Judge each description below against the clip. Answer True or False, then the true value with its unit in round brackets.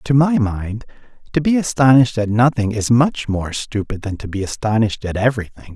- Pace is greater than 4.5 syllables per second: True (5.5 syllables/s)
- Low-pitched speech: True (115 Hz)